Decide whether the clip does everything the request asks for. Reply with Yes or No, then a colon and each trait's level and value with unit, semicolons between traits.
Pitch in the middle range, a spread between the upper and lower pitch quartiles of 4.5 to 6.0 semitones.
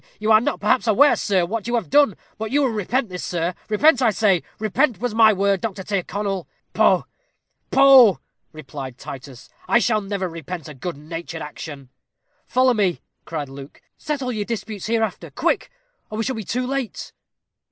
No: high, 210 Hz; wide, 5.5 semitones